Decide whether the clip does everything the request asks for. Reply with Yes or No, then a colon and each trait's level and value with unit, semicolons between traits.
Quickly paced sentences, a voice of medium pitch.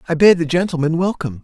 Yes: fast, 210 wpm; medium, 165 Hz